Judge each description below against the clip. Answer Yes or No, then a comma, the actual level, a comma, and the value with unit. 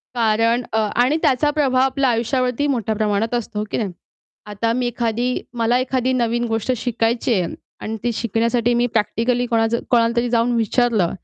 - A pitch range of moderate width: No, narrow, 1.8 semitones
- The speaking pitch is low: No, high, 235 Hz